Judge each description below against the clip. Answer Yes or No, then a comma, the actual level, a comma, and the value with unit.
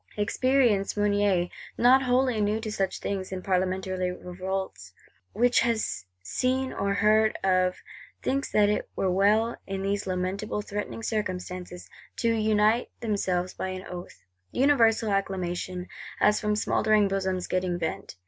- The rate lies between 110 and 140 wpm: Yes, slow, 135 wpm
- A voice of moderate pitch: No, high, 200 Hz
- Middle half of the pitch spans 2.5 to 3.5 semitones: Yes, average, 2.9 semitones